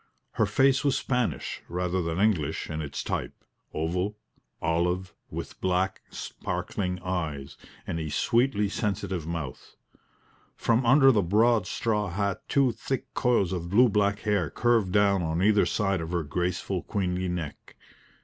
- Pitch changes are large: No, average, 3.7 semitones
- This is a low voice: Yes, very low, 95 Hz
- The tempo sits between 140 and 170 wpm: Yes, average, 145 wpm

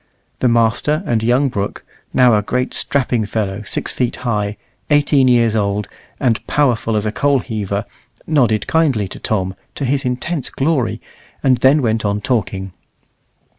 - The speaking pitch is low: Yes, low, 115 Hz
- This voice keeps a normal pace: Yes, average, 155 wpm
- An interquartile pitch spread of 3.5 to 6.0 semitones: Yes, average, 4.0 semitones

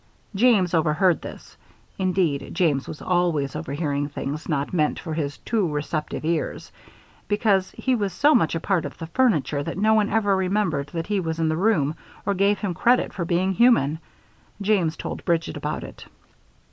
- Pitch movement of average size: Yes, average, 4.7 semitones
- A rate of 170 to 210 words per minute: Yes, average, 175 wpm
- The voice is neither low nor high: Yes, medium, 175 Hz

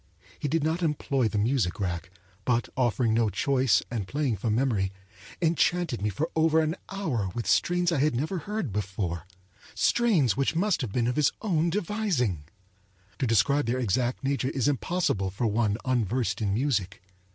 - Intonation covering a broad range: Yes, wide, 6.9 semitones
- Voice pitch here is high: No, low, 125 Hz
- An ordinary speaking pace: Yes, average, 170 wpm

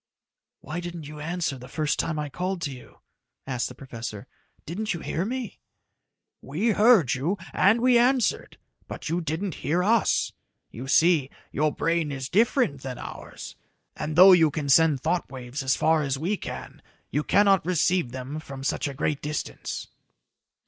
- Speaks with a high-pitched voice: No, medium, 155 Hz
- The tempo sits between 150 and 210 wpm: Yes, average, 170 wpm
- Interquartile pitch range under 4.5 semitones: No, average, 4.9 semitones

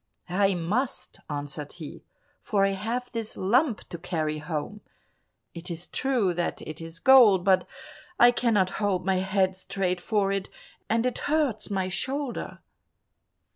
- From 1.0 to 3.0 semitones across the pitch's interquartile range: No, average, 4.5 semitones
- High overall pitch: Yes, high, 195 Hz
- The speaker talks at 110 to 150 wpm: Yes, average, 145 wpm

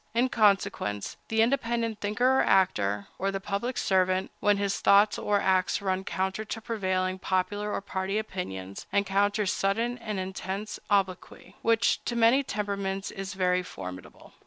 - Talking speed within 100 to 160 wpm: Yes, average, 150 wpm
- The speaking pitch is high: Yes, high, 200 Hz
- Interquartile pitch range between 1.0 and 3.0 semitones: Yes, narrow, 2.4 semitones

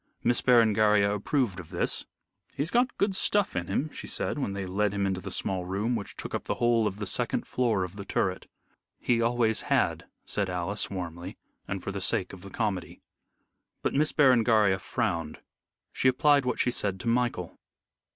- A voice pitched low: Yes, low, 105 Hz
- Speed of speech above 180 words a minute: Yes, average, 190 wpm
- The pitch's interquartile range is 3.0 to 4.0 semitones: No, average, 4.4 semitones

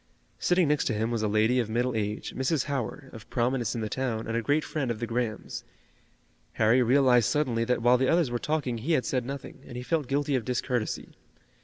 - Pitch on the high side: No, low, 125 Hz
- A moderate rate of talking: No, fast, 220 wpm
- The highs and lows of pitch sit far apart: No, average, 3.1 semitones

